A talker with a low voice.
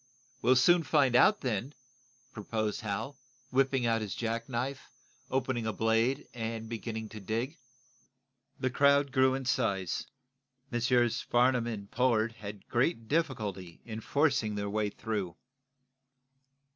Yes: low, 115 Hz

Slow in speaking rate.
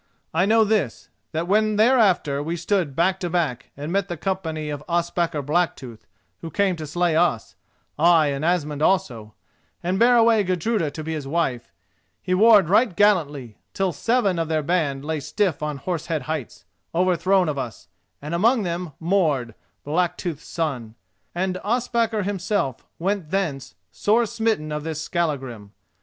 No: average, 155 wpm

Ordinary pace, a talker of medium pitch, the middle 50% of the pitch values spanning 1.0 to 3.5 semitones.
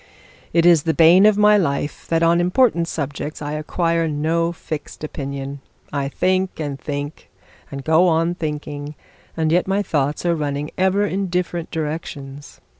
Yes: average, 160 wpm; medium, 160 Hz; average, 3.1 semitones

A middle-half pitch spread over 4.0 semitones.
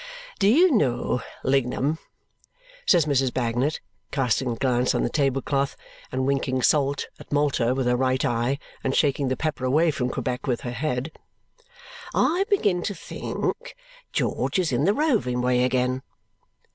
No: average, 3.5 semitones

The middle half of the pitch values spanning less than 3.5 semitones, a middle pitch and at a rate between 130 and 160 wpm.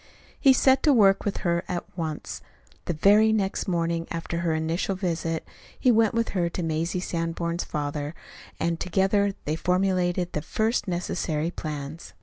Yes: average, 2.9 semitones; medium, 175 Hz; average, 155 wpm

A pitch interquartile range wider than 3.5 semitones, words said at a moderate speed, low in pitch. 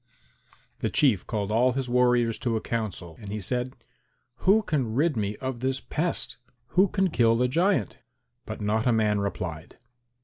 Yes: average, 3.9 semitones; average, 170 wpm; low, 120 Hz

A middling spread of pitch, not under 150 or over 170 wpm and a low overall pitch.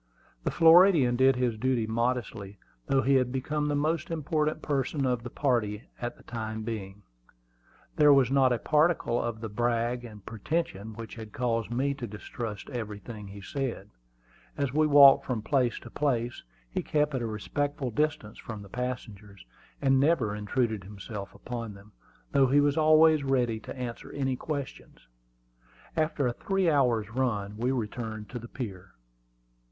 Yes: average, 4.3 semitones; average, 165 wpm; low, 125 Hz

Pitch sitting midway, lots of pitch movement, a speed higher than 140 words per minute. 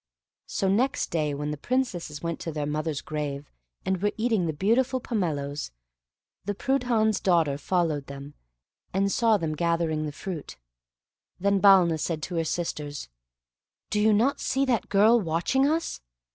Yes: medium, 175 Hz; wide, 6.1 semitones; average, 155 wpm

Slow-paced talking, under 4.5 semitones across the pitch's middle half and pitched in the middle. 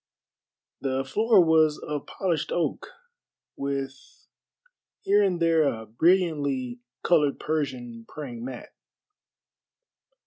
Yes: slow, 95 wpm; average, 4.0 semitones; medium, 145 Hz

